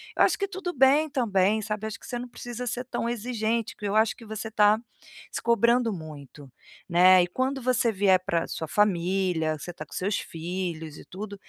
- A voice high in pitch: Yes, high, 210 Hz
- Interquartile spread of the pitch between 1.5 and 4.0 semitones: No, average, 4.8 semitones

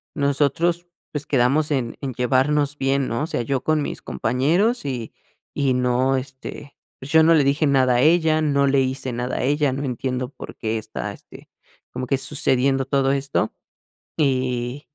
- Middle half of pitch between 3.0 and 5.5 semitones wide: No, narrow, 2.4 semitones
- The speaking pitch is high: No, low, 135 Hz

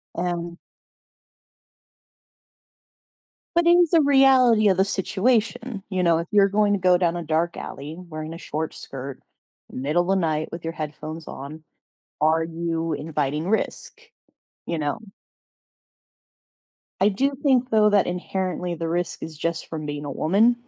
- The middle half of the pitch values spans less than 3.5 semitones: No, average, 4.6 semitones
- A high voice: No, medium, 175 Hz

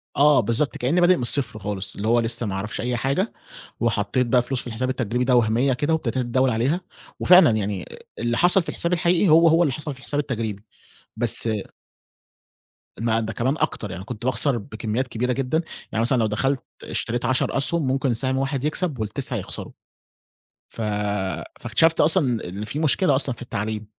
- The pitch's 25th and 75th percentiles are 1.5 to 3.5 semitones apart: No, average, 4.1 semitones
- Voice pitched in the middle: No, low, 125 Hz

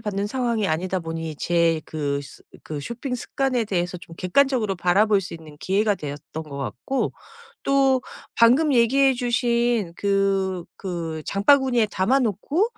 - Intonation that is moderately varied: No, wide, 6.5 semitones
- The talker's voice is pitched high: Yes, high, 200 Hz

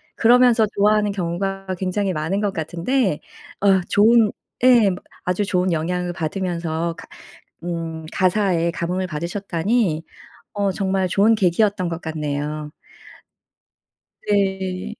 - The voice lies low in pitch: No, medium, 185 Hz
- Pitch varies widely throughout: No, average, 3.2 semitones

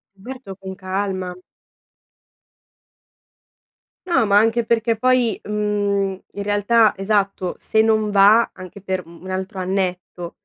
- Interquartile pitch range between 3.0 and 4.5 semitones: No, narrow, 2.6 semitones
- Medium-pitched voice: No, high, 200 Hz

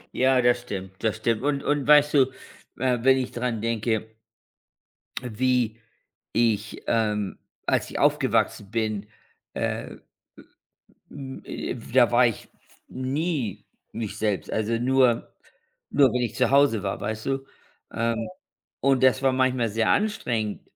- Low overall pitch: Yes, low, 120 Hz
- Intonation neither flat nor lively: Yes, average, 3.1 semitones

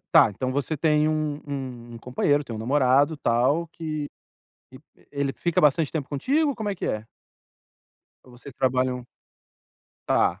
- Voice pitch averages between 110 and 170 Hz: Yes, medium, 140 Hz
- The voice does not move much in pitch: No, average, 3.4 semitones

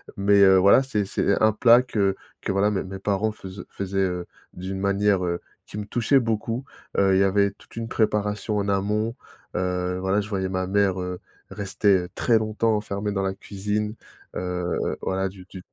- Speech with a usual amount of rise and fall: No, narrow, 1.9 semitones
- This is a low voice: Yes, low, 100 Hz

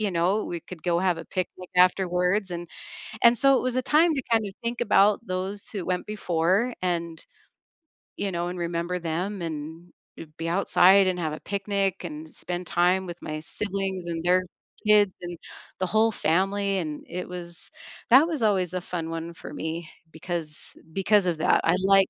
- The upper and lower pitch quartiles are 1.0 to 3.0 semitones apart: Yes, average, 2.7 semitones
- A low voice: No, medium, 180 Hz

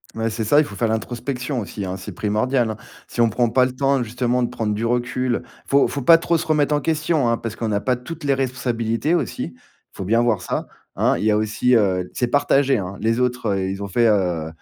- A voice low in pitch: Yes, low, 120 Hz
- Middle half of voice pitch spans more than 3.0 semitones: Yes, average, 3.5 semitones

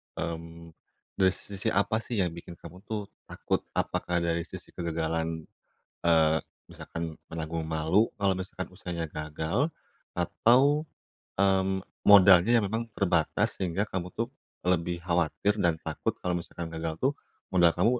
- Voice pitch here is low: Yes, very low, 90 Hz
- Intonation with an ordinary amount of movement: Yes, average, 3.1 semitones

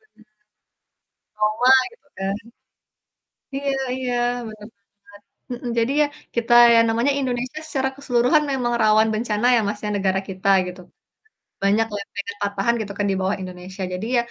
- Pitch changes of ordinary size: Yes, average, 3.6 semitones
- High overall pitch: Yes, high, 220 Hz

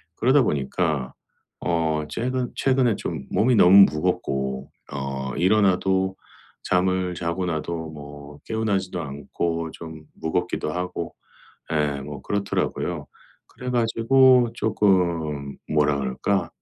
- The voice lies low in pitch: Yes, very low, 85 Hz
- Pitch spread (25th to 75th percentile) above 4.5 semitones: Yes, average, 5.3 semitones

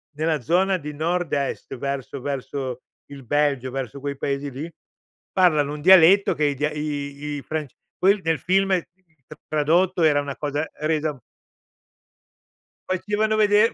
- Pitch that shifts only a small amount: No, average, 4.1 semitones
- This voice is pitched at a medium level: Yes, medium, 150 Hz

